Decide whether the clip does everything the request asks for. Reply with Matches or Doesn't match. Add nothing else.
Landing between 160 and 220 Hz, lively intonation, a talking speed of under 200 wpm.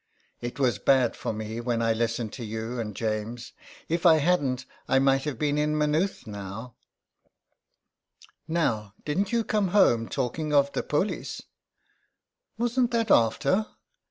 Doesn't match